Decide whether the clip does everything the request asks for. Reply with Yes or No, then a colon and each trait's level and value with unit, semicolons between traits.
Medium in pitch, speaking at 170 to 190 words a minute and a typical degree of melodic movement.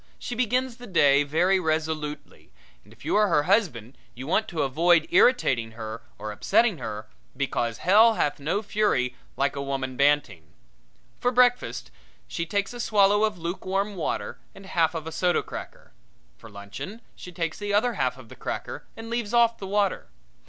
No: medium, 170 Hz; average, 175 wpm; wide, 7.2 semitones